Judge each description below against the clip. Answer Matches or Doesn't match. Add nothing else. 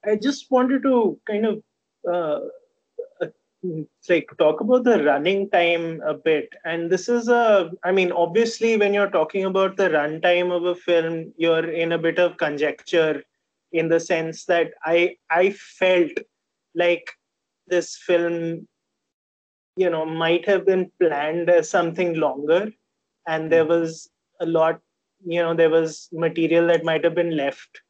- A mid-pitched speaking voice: Matches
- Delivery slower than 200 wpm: Matches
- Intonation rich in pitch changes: Doesn't match